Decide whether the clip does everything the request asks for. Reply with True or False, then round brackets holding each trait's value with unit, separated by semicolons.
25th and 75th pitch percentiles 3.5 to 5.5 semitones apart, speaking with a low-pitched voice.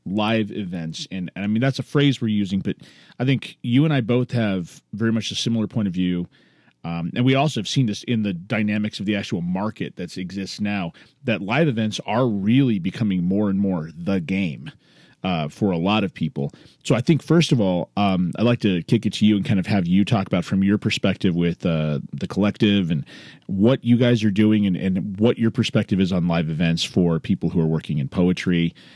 True (3.9 semitones; 100 Hz)